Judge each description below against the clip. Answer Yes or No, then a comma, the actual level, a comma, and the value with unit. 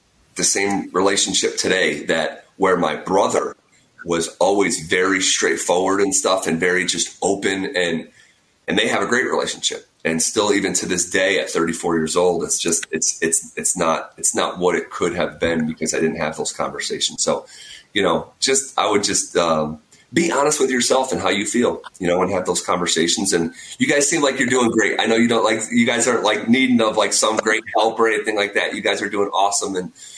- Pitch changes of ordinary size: No, wide, 8.9 semitones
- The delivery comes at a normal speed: No, fast, 215 wpm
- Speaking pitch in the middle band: No, very low, 95 Hz